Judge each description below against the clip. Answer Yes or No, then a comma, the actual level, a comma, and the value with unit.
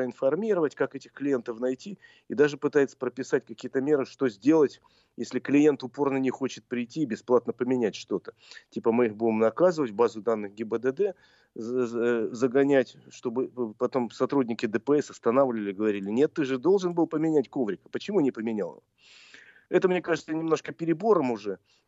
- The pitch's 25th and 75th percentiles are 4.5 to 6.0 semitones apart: No, average, 3.6 semitones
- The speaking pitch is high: No, low, 130 Hz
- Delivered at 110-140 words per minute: No, average, 150 wpm